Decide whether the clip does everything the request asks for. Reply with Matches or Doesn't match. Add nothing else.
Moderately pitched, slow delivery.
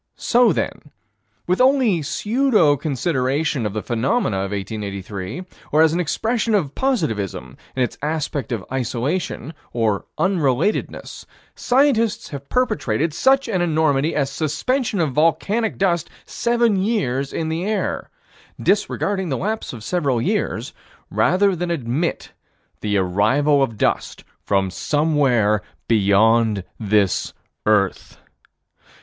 Matches